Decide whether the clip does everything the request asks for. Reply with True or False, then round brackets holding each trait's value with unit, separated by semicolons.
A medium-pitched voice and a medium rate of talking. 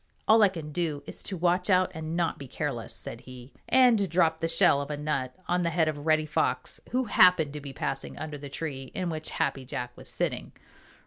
False (160 Hz; 220 wpm)